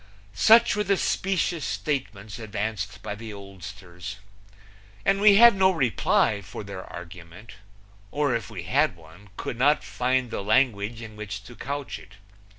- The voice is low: Yes, low, 110 Hz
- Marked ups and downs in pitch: Yes, wide, 6.0 semitones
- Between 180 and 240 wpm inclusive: No, average, 155 wpm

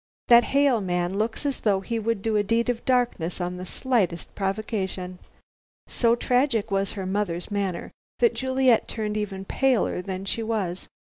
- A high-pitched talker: Yes, high, 210 Hz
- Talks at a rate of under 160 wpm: No, average, 165 wpm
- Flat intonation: No, average, 3.7 semitones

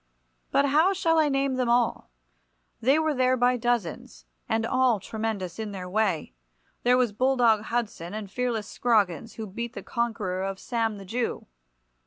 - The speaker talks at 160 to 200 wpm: Yes, average, 165 wpm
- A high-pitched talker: Yes, high, 230 Hz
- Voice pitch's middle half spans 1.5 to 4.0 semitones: Yes, average, 3.6 semitones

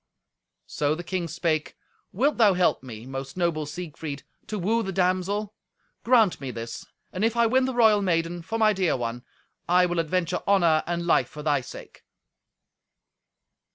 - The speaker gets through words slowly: No, average, 165 wpm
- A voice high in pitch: No, medium, 175 Hz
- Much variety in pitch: No, average, 4.9 semitones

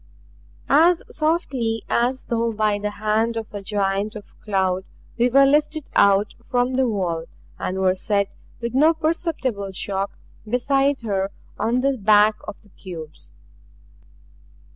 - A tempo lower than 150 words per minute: Yes, average, 140 wpm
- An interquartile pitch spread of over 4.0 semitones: Yes, average, 4.7 semitones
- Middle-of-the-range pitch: No, high, 215 Hz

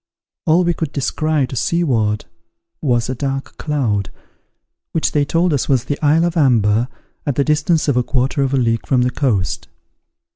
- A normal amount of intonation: Yes, average, 3.9 semitones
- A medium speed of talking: Yes, average, 180 wpm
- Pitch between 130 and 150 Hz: Yes, low, 135 Hz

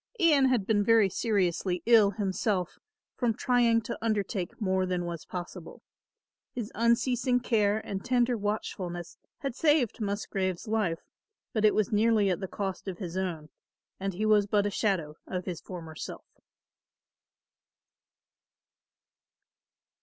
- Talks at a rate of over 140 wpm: No, slow, 135 wpm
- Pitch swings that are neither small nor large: Yes, average, 3.7 semitones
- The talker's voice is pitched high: Yes, high, 205 Hz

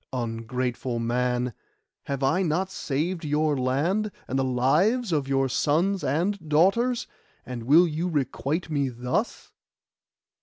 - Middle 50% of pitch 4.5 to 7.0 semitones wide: Yes, wide, 5.6 semitones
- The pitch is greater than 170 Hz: No, medium, 145 Hz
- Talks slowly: Yes, slow, 125 wpm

